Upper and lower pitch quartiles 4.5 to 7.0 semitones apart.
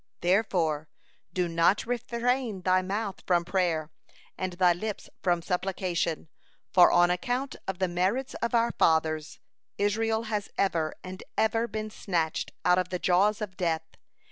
No: average, 3.6 semitones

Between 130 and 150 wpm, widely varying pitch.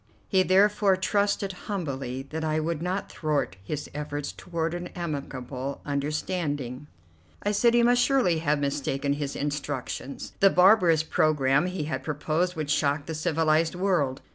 No: average, 145 wpm; average, 4.2 semitones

